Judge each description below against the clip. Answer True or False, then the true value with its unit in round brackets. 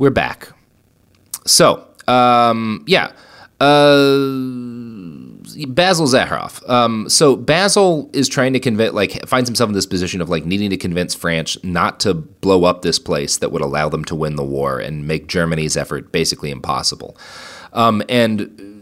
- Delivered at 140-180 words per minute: True (155 wpm)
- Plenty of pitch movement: True (6.8 semitones)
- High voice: False (115 Hz)